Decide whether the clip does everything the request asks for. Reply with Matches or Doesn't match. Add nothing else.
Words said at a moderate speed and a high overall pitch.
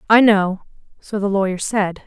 Matches